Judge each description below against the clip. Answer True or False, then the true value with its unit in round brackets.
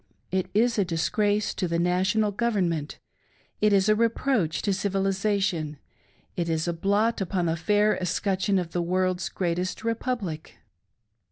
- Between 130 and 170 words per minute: True (145 wpm)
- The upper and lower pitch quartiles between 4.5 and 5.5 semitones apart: False (3.4 semitones)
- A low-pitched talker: False (190 Hz)